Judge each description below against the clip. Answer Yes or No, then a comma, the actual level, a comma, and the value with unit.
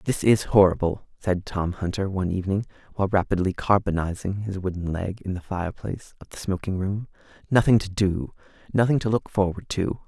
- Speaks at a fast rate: No, average, 175 wpm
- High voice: No, very low, 95 Hz